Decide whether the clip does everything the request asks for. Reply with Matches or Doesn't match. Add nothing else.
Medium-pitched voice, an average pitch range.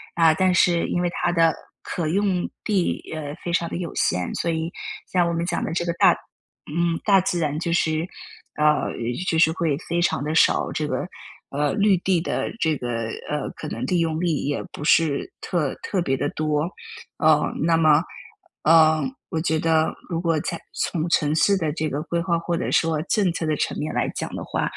Doesn't match